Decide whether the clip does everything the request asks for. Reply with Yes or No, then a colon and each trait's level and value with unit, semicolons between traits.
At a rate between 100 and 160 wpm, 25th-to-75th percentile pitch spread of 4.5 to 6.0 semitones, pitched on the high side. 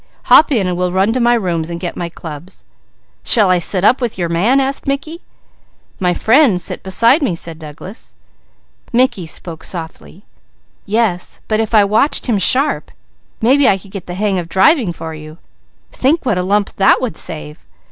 No: average, 185 wpm; wide, 5.5 semitones; high, 195 Hz